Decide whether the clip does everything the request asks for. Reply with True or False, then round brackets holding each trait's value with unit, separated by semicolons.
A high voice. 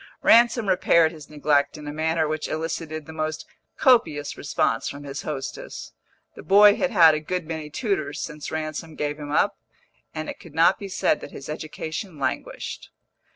False (155 Hz)